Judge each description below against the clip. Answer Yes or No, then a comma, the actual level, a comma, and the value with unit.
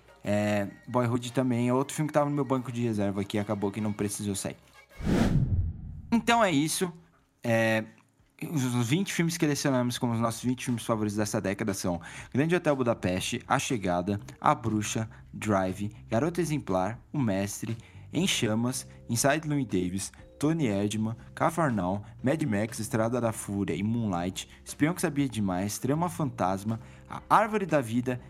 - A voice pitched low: Yes, low, 115 Hz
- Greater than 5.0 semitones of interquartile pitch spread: Yes, wide, 5.5 semitones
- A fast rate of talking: No, average, 155 wpm